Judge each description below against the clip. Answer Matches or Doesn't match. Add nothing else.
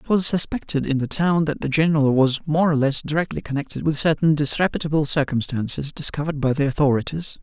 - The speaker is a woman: Doesn't match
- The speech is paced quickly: Doesn't match